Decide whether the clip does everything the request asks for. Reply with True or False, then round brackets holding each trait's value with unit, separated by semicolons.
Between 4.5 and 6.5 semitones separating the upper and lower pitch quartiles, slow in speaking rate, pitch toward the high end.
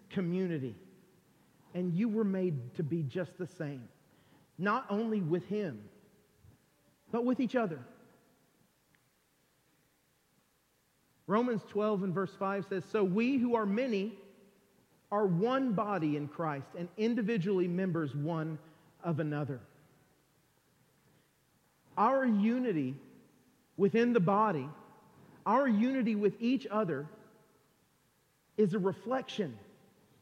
True (5.4 semitones; 105 wpm; 195 Hz)